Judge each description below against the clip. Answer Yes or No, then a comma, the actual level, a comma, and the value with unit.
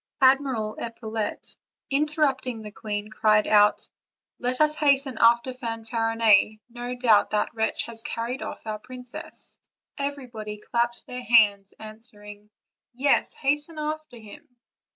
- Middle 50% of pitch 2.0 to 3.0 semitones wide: No, average, 3.4 semitones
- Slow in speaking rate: Yes, slow, 120 wpm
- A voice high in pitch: Yes, high, 235 Hz